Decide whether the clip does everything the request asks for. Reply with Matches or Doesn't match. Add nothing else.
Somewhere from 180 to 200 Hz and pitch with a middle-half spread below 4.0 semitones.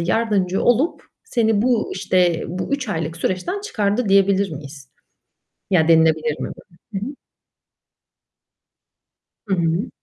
Doesn't match